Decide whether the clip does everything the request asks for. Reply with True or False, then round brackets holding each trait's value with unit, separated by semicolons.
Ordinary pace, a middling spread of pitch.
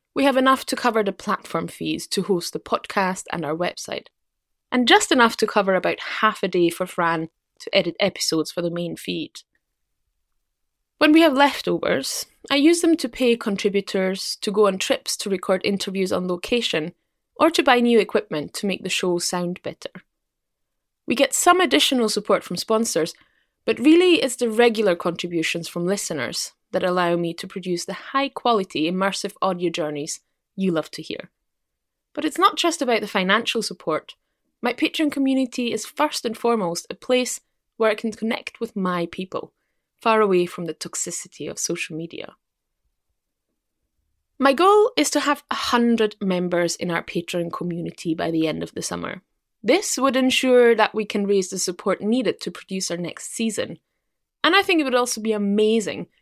False (175 wpm; 5.8 semitones)